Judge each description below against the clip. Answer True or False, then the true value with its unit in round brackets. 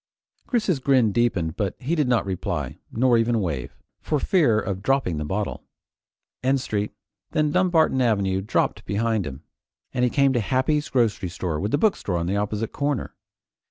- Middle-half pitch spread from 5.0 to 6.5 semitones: True (5.6 semitones)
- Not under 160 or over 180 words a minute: True (165 wpm)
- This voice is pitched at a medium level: False (115 Hz)